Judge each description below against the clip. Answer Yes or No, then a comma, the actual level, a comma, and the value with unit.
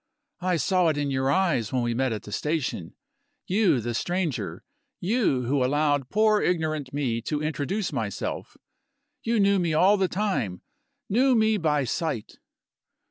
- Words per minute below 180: Yes, average, 155 wpm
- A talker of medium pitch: Yes, medium, 155 Hz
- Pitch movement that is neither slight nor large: No, wide, 6.4 semitones